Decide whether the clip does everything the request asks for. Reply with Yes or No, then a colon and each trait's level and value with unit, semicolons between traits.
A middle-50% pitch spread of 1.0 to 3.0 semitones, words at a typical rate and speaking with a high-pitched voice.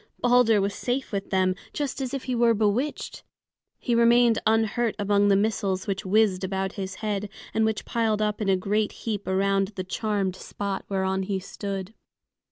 Yes: narrow, 2.5 semitones; average, 175 wpm; high, 205 Hz